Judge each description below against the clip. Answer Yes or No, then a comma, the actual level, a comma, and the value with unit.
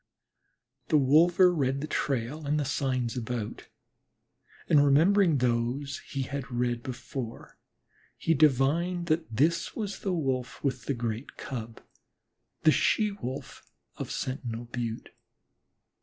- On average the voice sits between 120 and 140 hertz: Yes, low, 135 Hz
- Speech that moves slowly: Yes, slow, 125 wpm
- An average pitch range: Yes, average, 4.2 semitones